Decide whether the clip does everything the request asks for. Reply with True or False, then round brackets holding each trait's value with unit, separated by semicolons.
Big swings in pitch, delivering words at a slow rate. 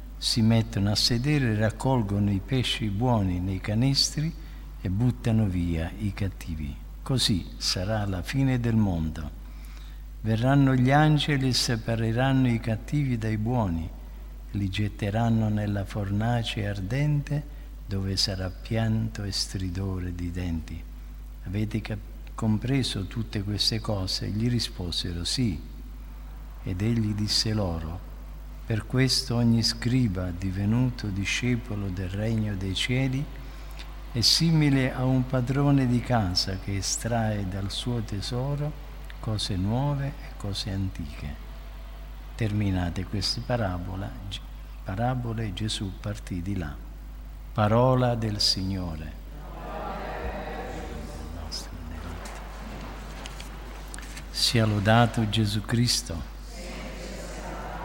False (4.4 semitones; 100 wpm)